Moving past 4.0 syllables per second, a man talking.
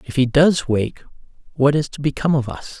Yes: 5.5 syllables/s; male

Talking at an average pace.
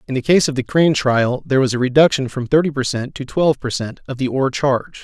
No: fast, 275 wpm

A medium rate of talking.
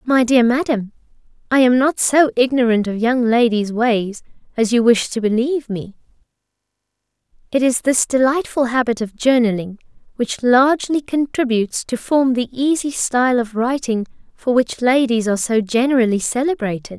Yes: average, 150 wpm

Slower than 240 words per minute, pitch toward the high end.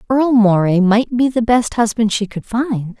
Yes: average, 200 wpm; high, 225 Hz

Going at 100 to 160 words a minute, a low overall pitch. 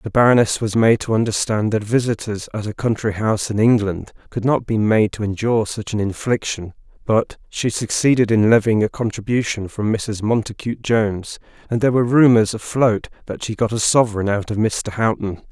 No: average, 185 wpm; low, 110 Hz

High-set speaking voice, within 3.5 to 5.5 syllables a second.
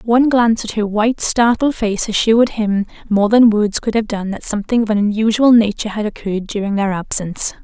No: high, 215 Hz; 5.9 syllables/s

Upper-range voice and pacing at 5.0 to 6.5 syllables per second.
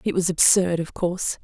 No: medium, 180 Hz; 5.4 syllables/s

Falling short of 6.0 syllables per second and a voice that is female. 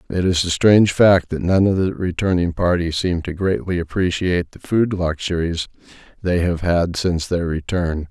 No: 4.9 syllables/s; male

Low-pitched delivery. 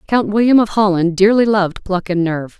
No: high, 195 Hz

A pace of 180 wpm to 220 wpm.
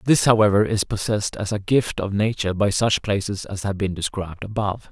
Yes: fast, 205 wpm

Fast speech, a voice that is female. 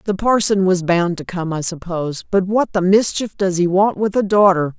Yes: fast, 225 wpm; female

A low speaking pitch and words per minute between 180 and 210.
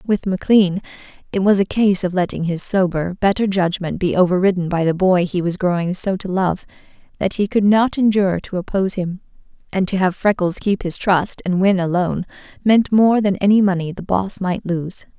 No: high, 190 Hz; average, 200 wpm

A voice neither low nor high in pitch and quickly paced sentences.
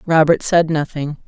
No: medium, 155 Hz; average, 140 wpm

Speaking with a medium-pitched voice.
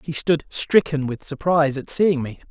Yes: medium, 150 Hz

